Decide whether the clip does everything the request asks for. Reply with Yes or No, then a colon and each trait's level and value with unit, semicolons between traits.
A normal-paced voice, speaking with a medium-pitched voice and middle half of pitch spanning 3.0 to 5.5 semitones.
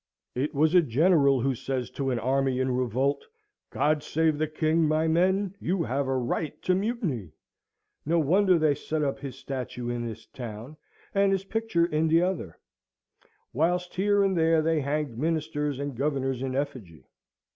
Yes: average, 165 wpm; medium, 150 Hz; average, 4.1 semitones